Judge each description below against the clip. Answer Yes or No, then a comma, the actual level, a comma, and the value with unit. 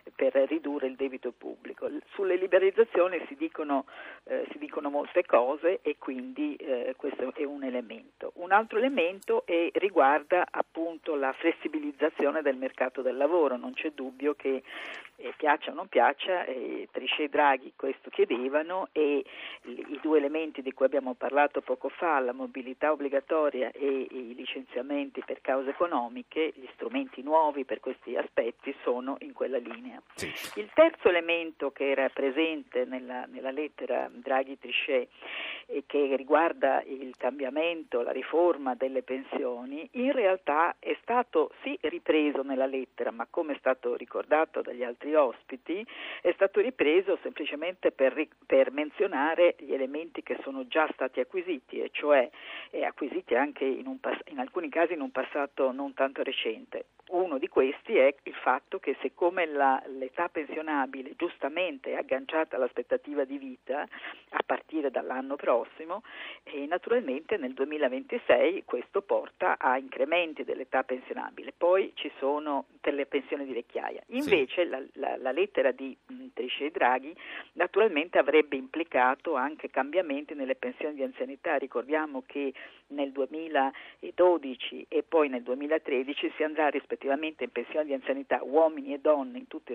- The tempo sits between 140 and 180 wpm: Yes, average, 145 wpm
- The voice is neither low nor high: Yes, medium, 160 Hz